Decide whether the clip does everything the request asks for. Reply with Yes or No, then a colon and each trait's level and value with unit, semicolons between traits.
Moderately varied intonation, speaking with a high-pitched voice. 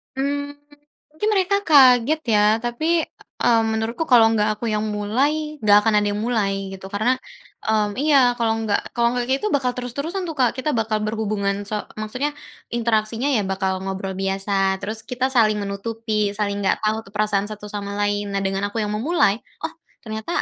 Yes: average, 3.7 semitones; high, 220 Hz